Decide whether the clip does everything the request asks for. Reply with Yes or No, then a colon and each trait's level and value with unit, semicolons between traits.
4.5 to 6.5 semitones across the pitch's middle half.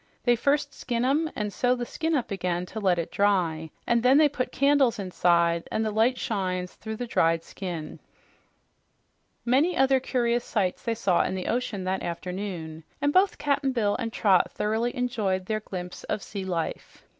Yes: wide, 5.4 semitones